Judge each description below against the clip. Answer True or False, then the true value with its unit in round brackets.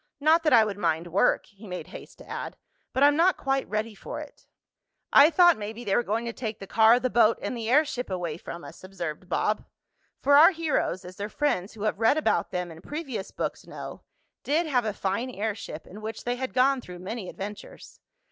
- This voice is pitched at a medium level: False (220 Hz)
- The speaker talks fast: True (215 wpm)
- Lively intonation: True (5.7 semitones)